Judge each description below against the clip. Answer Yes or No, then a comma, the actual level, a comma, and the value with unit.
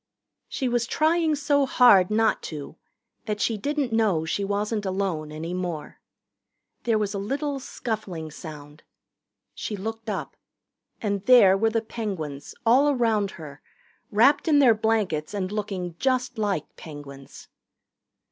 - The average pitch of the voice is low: No, high, 210 Hz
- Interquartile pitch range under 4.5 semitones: No, average, 5.0 semitones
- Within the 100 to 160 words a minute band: Yes, average, 140 wpm